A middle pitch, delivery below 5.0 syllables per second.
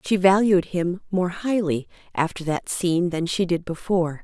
Yes: medium, 180 Hz; 4.8 syllables/s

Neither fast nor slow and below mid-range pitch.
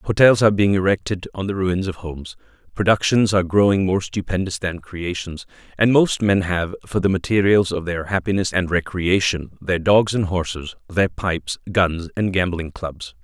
Yes: average, 170 wpm; very low, 95 Hz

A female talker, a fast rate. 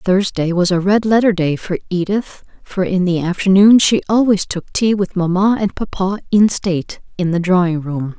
No: female; average, 190 wpm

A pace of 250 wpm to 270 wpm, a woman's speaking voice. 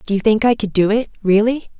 Yes: fast, 265 wpm; female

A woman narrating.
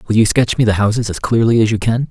No: male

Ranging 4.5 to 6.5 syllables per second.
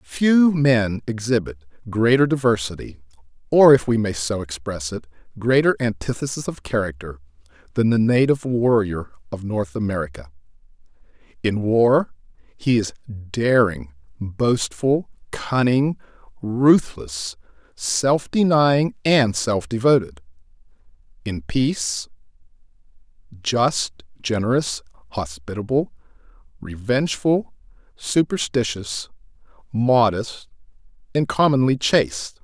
No: 4.0 syllables/s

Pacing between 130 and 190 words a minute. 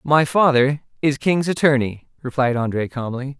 Yes: average, 140 wpm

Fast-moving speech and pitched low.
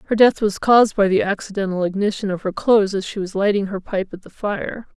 No: fast, 240 wpm; high, 200 Hz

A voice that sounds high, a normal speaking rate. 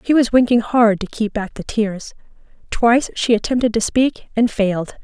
Yes: high, 225 Hz; average, 190 wpm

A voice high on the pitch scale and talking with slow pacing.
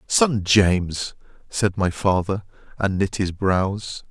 No: very low, 95 Hz; slow, 130 wpm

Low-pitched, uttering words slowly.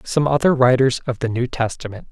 No: low, 130 Hz; average, 200 wpm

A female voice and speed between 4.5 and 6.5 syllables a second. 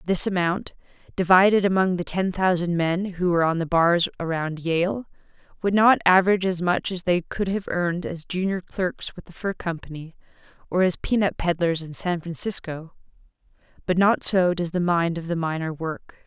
Yes: female; 5.1 syllables/s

